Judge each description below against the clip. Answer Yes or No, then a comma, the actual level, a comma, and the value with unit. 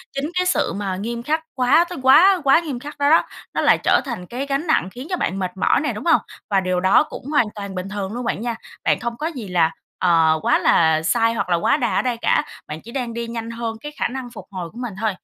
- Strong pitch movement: Yes, wide, 6.5 semitones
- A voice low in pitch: No, high, 235 Hz